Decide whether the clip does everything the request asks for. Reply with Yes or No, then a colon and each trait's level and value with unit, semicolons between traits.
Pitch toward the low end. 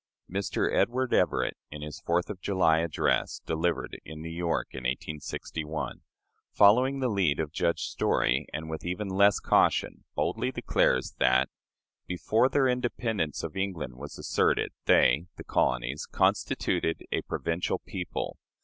Yes: very low, 85 Hz